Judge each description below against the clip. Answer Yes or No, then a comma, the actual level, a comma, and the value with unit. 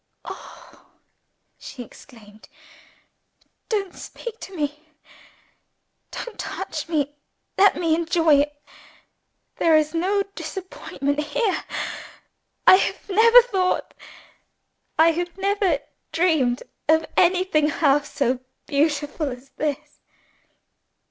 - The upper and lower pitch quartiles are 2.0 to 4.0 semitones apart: No, average, 4.4 semitones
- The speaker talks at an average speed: No, slow, 95 wpm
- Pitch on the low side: No, very high, 320 Hz